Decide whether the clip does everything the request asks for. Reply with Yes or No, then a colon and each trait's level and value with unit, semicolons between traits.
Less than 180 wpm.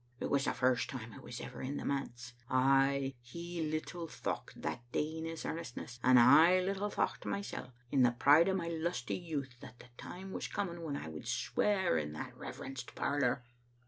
No: average, 195 wpm